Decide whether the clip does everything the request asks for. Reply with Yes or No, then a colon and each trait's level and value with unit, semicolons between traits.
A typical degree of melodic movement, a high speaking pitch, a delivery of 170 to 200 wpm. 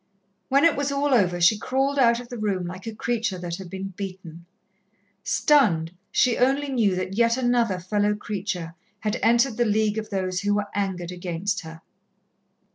Yes: average, 4.6 semitones; high, 205 Hz; average, 180 wpm